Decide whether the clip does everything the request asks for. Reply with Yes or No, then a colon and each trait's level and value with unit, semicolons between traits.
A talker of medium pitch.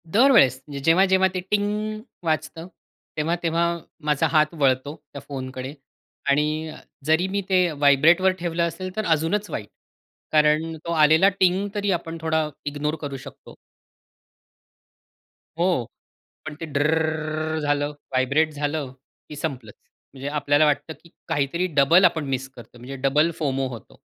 Yes: medium, 155 Hz